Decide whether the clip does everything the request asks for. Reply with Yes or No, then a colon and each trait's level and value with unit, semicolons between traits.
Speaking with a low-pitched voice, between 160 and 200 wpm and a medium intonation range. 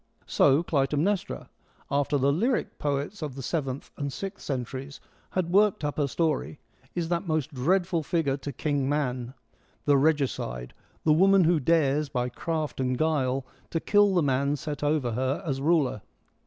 No: medium, 145 Hz; average, 170 wpm; average, 3.5 semitones